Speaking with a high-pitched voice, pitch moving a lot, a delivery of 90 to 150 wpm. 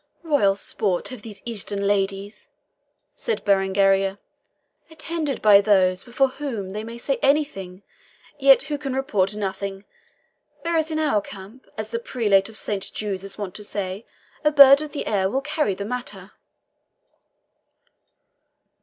Yes: high, 210 Hz; wide, 5.7 semitones; average, 145 wpm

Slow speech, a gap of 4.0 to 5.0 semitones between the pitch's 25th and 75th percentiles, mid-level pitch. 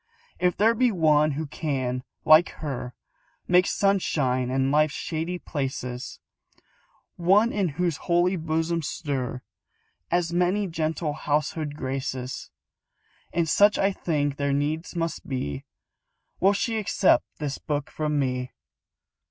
Yes: slow, 125 wpm; average, 4.4 semitones; medium, 155 Hz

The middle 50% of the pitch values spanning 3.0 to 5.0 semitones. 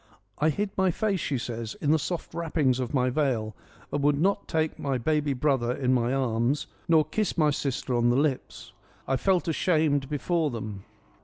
Yes: average, 4.0 semitones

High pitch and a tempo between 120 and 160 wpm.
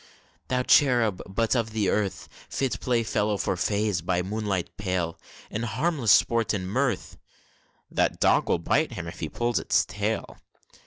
No: low, 105 Hz; average, 150 wpm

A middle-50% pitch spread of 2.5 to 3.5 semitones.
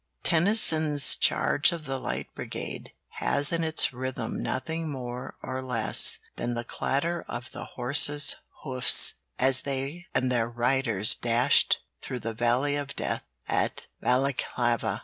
Yes: average, 3.2 semitones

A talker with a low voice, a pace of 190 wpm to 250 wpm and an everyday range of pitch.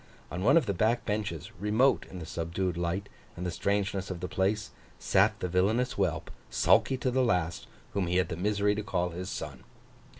Yes: very low, 95 Hz; average, 200 wpm; average, 3.1 semitones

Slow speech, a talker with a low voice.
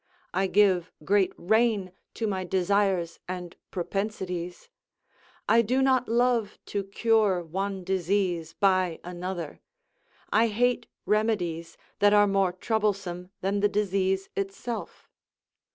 No: slow, 115 wpm; high, 195 Hz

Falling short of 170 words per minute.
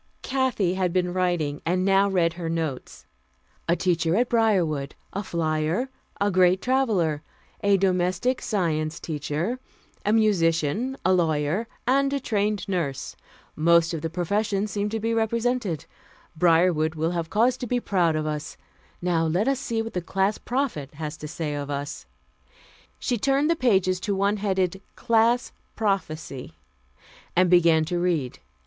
Yes: average, 155 wpm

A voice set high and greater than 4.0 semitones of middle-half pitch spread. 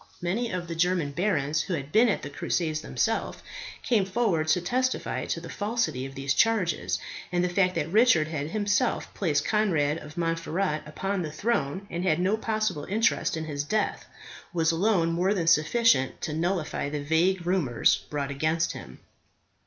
No: medium, 170 Hz; average, 4.8 semitones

